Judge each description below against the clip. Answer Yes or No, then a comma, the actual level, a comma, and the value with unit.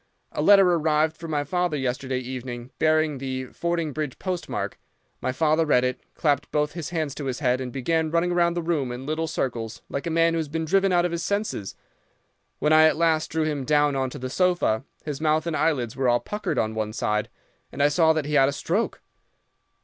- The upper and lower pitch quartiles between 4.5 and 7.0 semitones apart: No, average, 4.0 semitones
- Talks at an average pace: No, fast, 220 wpm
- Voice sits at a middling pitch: Yes, medium, 150 Hz